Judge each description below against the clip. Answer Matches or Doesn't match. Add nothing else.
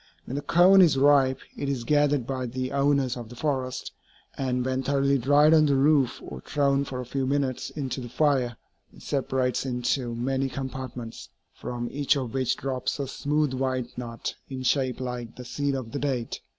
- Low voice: Matches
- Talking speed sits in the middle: Matches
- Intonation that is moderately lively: Doesn't match